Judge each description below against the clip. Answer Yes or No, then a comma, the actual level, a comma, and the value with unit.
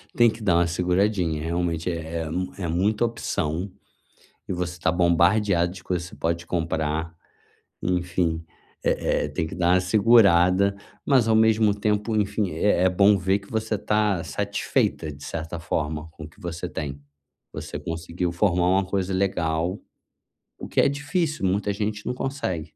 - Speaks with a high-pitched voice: No, very low, 90 Hz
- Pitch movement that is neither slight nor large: Yes, average, 3.5 semitones